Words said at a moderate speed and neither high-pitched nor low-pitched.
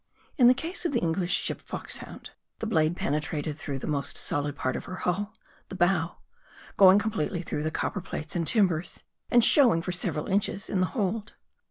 Yes: average, 195 wpm; medium, 180 Hz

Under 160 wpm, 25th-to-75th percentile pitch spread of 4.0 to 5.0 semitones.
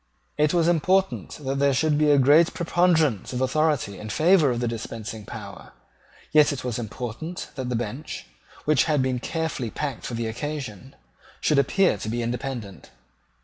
No: average, 170 wpm; average, 4.6 semitones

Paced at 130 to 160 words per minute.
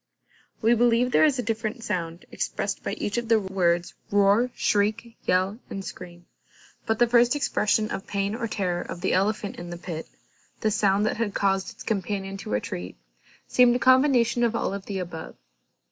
No: average, 180 wpm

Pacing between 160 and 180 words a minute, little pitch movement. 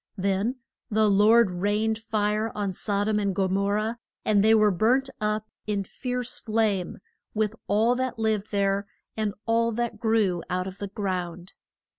Yes: average, 165 wpm; narrow, 2.0 semitones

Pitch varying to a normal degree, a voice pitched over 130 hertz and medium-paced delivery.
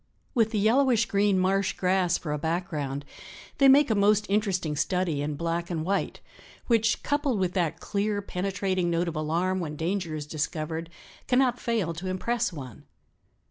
Yes: average, 4.2 semitones; medium, 185 Hz; average, 165 wpm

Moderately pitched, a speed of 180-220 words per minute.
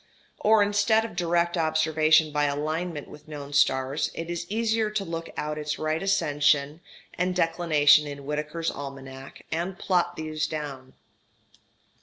No: medium, 155 Hz; average, 140 wpm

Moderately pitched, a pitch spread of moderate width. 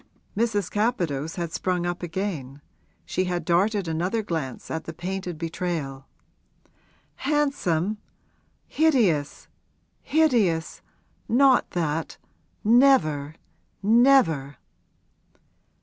No: medium, 180 Hz; wide, 5.7 semitones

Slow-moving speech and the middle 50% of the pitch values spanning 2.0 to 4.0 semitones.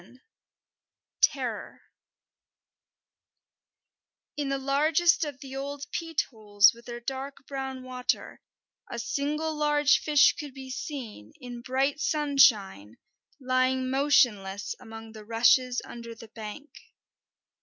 Yes: slow, 110 wpm; average, 3.7 semitones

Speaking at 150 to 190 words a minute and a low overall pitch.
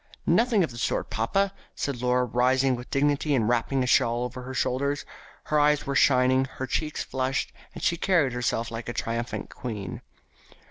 Yes: average, 180 wpm; low, 130 Hz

